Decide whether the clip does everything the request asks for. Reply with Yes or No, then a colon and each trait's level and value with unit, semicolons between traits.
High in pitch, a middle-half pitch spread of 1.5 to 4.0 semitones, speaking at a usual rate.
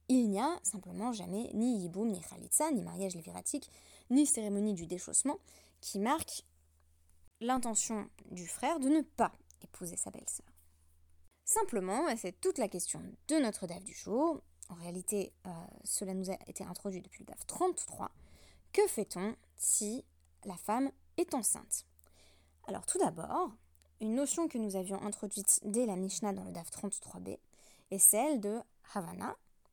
No: high, 205 Hz; wide, 5.6 semitones; average, 155 wpm